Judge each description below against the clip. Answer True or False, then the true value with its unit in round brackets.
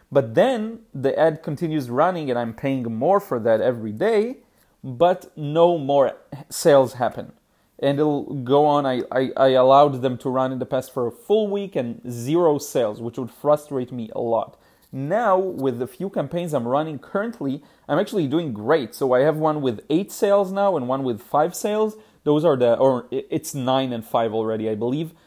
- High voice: False (140 Hz)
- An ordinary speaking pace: True (195 wpm)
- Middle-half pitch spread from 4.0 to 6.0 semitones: True (4.7 semitones)